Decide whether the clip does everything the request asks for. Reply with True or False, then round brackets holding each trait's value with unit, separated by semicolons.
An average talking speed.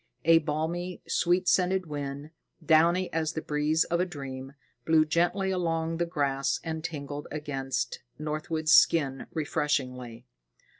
False (130 wpm)